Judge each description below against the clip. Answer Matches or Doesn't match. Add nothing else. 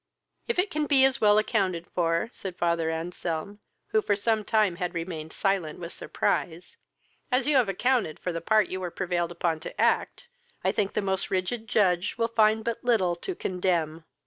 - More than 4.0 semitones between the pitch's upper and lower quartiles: Matches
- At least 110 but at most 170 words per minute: Doesn't match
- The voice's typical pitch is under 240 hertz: Matches